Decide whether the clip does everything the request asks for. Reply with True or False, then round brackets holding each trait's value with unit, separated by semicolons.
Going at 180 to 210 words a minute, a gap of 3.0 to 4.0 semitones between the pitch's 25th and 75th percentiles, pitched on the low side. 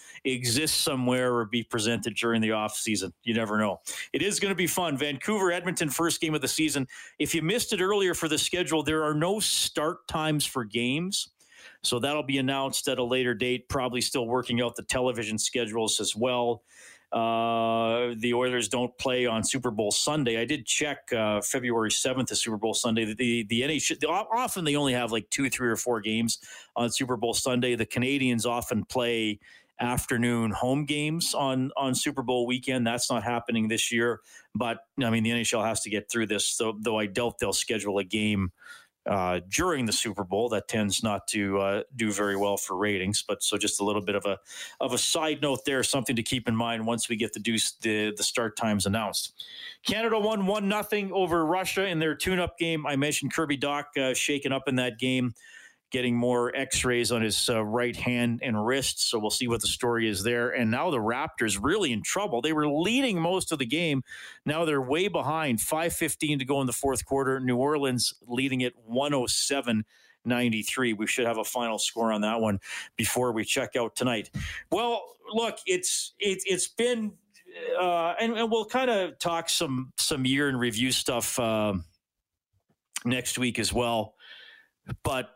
False (200 wpm; 4.7 semitones; 125 Hz)